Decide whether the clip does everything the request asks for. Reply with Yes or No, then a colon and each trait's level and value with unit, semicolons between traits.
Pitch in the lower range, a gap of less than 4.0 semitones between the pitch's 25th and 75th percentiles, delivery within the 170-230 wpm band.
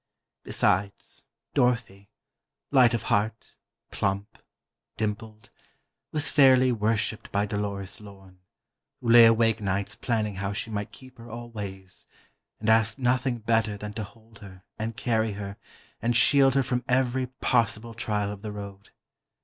No: low, 110 Hz; average, 2.8 semitones; slow, 135 wpm